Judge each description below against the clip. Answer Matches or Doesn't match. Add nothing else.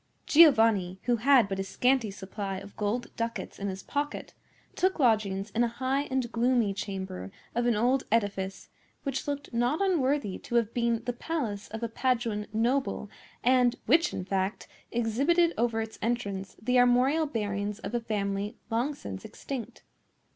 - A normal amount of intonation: Matches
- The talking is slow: Doesn't match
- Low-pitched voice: Doesn't match